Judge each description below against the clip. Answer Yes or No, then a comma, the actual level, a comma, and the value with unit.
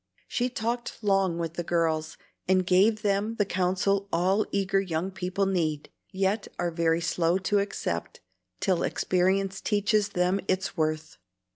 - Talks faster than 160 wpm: No, average, 145 wpm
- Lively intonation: No, average, 2.7 semitones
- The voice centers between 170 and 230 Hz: Yes, high, 190 Hz